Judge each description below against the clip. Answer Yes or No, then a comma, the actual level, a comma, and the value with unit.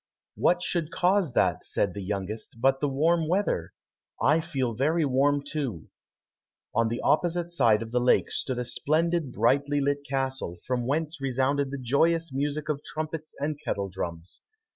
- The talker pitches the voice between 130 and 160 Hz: Yes, medium, 140 Hz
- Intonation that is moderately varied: Yes, average, 4.4 semitones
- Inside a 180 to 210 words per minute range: No, average, 165 wpm